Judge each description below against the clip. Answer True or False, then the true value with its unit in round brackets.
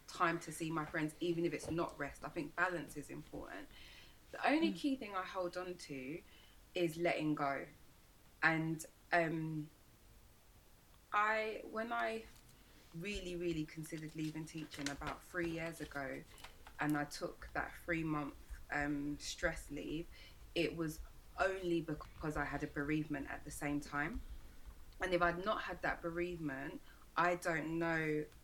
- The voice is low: False (160 Hz)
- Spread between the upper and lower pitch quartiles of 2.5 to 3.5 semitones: True (3.0 semitones)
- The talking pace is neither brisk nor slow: True (150 wpm)